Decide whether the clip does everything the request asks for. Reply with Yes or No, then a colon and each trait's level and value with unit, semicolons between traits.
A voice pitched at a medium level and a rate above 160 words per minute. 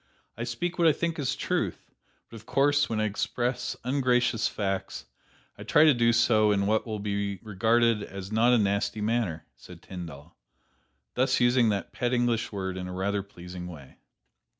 No: low, 110 Hz; average, 175 wpm